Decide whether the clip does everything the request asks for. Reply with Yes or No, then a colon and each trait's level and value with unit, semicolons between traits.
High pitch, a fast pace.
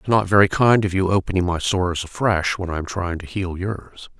No: very low, 95 Hz; fast, 255 wpm